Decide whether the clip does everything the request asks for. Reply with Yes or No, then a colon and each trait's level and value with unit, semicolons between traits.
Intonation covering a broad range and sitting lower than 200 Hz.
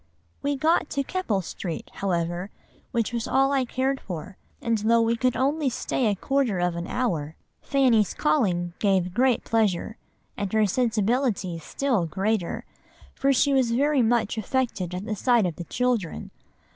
No: wide, 5.7 semitones; high, 225 Hz